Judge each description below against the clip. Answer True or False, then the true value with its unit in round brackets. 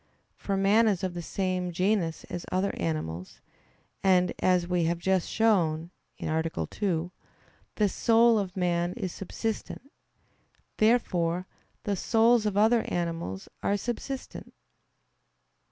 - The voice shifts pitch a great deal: False (3.8 semitones)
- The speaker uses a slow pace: True (120 wpm)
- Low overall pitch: False (185 Hz)